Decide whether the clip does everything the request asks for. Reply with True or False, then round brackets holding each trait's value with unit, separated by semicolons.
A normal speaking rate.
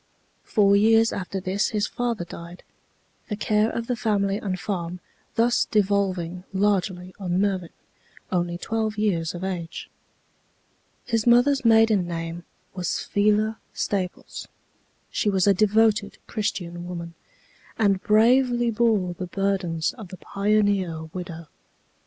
False (125 wpm)